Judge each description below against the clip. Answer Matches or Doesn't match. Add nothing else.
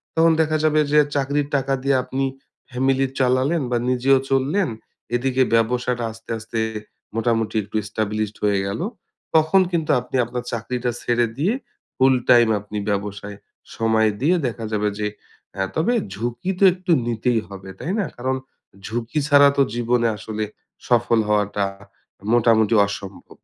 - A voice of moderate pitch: Doesn't match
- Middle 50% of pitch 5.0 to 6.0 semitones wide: Doesn't match